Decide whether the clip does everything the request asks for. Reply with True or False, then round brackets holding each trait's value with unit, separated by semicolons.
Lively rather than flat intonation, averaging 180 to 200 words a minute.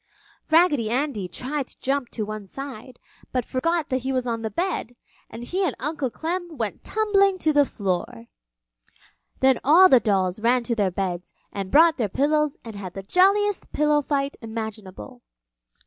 False (6.1 semitones; 170 wpm)